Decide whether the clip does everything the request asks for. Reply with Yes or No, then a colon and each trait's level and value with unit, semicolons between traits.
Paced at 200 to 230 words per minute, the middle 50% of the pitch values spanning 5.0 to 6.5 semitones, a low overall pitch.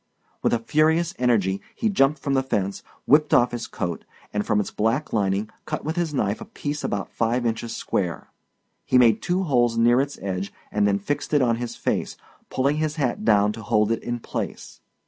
Yes: fast, 205 wpm; wide, 5.4 semitones; low, 120 Hz